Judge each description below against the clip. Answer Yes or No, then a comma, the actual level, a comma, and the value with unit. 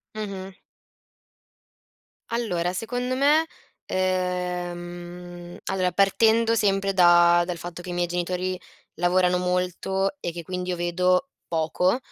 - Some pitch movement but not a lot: No, narrow, 1.8 semitones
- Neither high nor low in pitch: Yes, medium, 180 Hz